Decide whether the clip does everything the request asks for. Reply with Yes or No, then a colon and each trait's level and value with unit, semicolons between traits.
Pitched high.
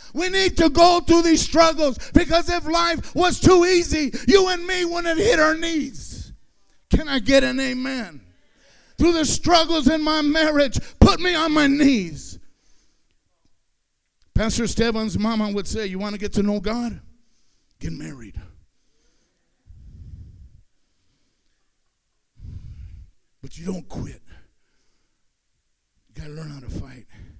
Yes: very high, 270 Hz